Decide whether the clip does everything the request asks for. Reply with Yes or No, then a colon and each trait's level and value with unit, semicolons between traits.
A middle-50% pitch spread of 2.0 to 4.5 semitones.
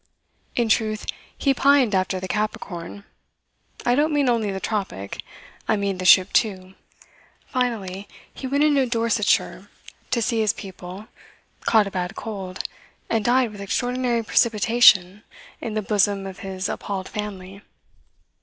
Yes: average, 3.6 semitones